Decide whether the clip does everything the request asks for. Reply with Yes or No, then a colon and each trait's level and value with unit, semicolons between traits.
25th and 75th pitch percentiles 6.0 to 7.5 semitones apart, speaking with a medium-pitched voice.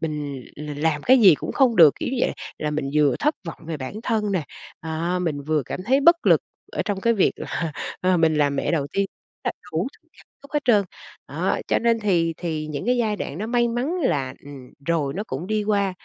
Yes: wide, 6.3 semitones; medium, 170 Hz